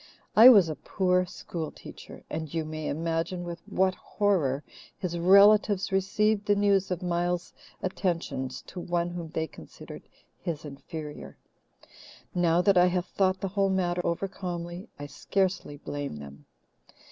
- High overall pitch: No, medium, 175 Hz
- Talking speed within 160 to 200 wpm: No, average, 145 wpm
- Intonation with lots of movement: No, average, 3.0 semitones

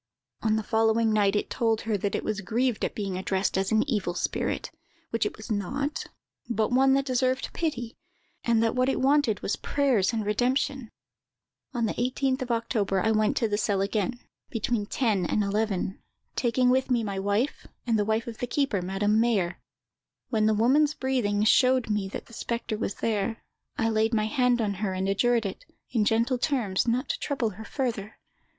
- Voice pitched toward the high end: Yes, high, 225 Hz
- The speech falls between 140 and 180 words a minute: No, average, 190 wpm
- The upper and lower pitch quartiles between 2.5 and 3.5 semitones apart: Yes, average, 3.2 semitones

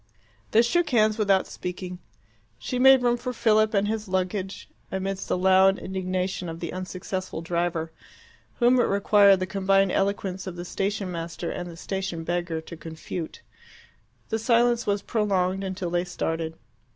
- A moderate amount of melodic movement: Yes, average, 3.0 semitones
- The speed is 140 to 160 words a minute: Yes, average, 155 wpm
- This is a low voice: No, high, 190 Hz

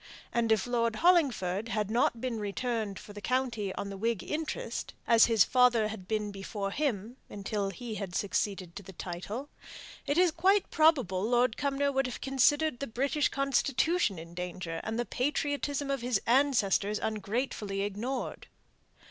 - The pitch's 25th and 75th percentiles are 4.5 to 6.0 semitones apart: Yes, average, 5.3 semitones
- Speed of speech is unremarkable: Yes, average, 160 wpm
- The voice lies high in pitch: Yes, high, 230 Hz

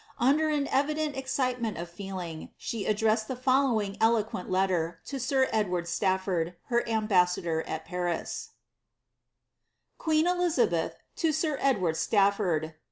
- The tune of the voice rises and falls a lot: Yes, wide, 7.0 semitones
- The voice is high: Yes, high, 215 Hz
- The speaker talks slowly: Yes, slow, 130 wpm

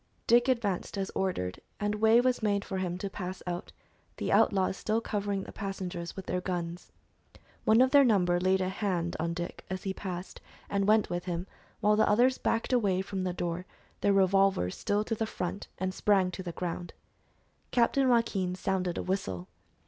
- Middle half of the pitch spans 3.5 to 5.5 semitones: No, average, 2.7 semitones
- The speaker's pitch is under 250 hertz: Yes, high, 190 Hz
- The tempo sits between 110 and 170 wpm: No, average, 185 wpm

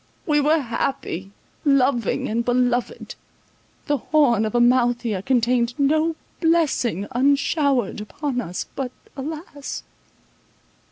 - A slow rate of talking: Yes, slow, 100 wpm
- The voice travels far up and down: No, average, 3.5 semitones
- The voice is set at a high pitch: Yes, very high, 255 Hz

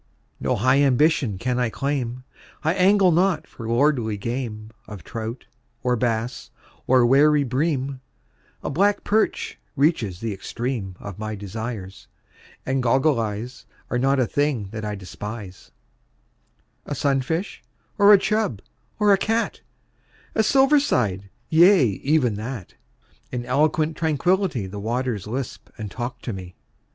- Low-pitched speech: Yes, low, 125 Hz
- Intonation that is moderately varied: No, wide, 5.8 semitones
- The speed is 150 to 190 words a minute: No, average, 140 wpm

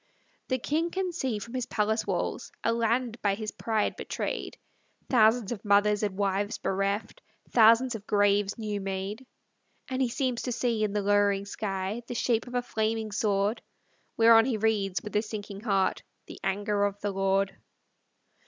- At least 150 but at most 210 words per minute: Yes, average, 170 wpm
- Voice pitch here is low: No, high, 215 Hz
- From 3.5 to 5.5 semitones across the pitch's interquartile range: No, narrow, 2.5 semitones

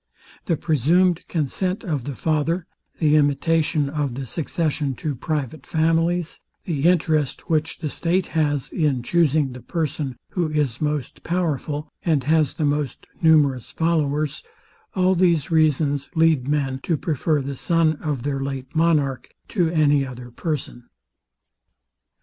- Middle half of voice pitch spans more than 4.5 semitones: No, average, 2.8 semitones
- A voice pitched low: No, medium, 150 Hz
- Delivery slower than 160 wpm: Yes, average, 140 wpm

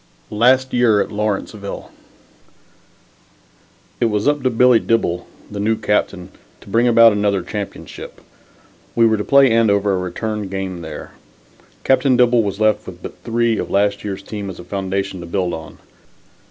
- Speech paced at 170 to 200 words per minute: No, average, 160 wpm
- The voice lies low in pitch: Yes, low, 105 Hz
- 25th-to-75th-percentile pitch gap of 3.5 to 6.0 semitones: No, average, 3.0 semitones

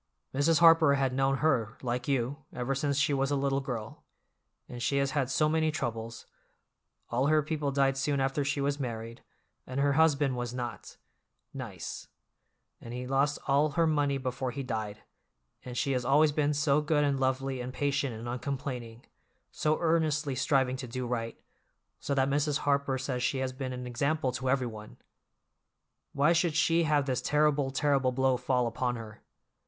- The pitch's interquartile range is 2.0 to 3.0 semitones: Yes, narrow, 2.4 semitones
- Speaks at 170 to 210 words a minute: Yes, average, 175 wpm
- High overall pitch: No, low, 135 Hz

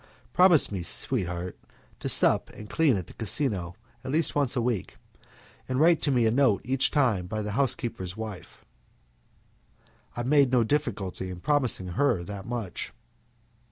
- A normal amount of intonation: No, wide, 6.1 semitones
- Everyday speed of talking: Yes, average, 155 wpm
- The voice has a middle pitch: No, low, 115 Hz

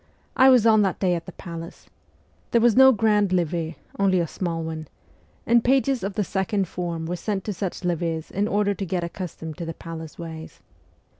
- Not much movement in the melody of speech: No, average, 3.9 semitones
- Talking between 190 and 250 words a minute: Yes, average, 200 wpm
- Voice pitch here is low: No, medium, 185 Hz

